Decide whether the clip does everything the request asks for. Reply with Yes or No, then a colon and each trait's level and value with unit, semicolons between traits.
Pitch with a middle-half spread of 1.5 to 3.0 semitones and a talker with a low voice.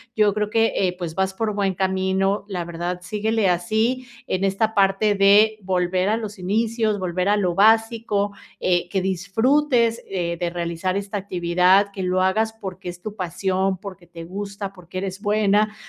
No: average, 2.7 semitones; high, 195 Hz